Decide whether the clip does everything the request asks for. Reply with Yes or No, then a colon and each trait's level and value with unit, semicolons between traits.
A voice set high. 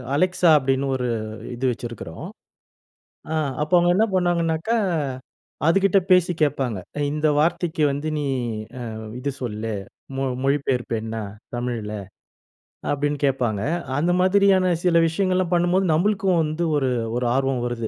No: medium, 150 Hz